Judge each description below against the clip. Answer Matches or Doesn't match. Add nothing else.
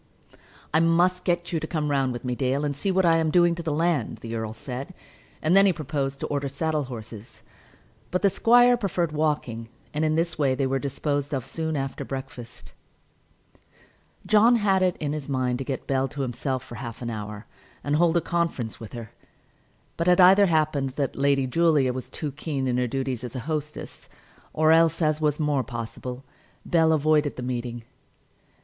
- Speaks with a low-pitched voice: Doesn't match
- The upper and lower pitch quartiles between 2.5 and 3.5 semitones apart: Doesn't match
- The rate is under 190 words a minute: Doesn't match